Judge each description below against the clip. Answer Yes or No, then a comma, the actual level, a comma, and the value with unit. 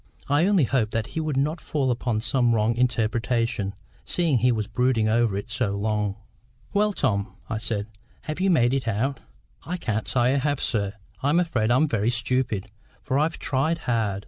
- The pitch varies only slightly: No, average, 4.4 semitones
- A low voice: Yes, low, 120 Hz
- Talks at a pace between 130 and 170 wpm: No, average, 185 wpm